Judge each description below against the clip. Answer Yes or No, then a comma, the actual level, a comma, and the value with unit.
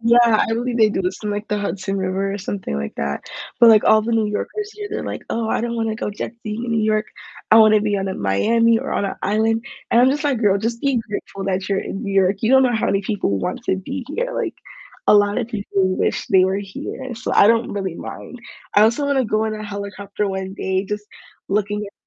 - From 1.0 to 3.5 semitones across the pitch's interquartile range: Yes, average, 2.8 semitones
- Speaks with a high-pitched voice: Yes, high, 210 Hz